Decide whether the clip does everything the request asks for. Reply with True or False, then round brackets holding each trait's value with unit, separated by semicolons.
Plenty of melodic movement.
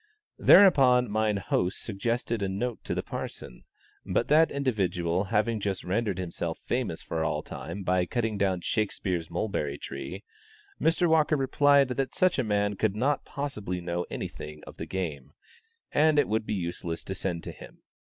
True (5.9 semitones)